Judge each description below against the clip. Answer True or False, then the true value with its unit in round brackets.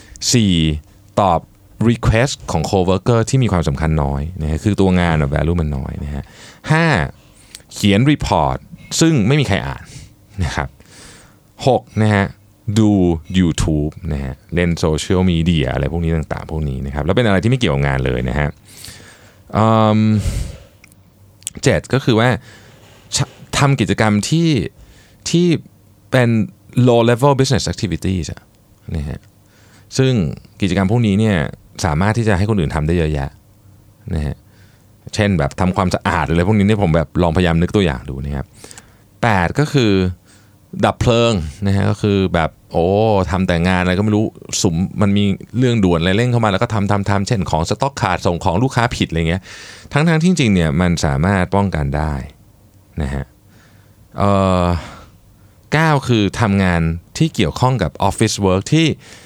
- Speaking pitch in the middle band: False (100 Hz)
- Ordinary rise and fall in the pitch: True (4.4 semitones)